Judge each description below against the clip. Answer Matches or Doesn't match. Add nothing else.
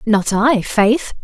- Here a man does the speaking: Doesn't match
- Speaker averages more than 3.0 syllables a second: Doesn't match